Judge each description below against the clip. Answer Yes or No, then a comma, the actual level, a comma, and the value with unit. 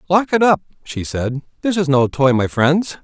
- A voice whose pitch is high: No, medium, 155 Hz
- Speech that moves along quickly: Yes, fast, 215 wpm